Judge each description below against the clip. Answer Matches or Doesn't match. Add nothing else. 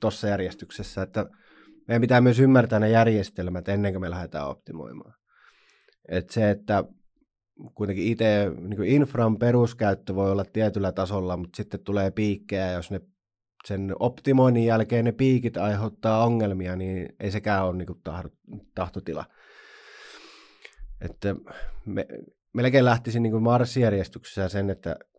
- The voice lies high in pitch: Doesn't match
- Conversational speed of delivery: Matches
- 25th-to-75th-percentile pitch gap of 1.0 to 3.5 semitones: Matches